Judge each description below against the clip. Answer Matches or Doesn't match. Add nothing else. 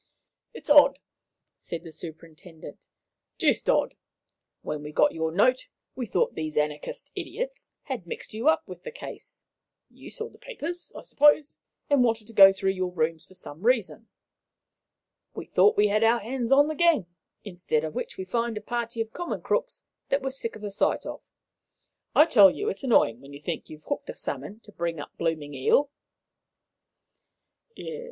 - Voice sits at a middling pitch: Doesn't match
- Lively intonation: Matches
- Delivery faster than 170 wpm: Matches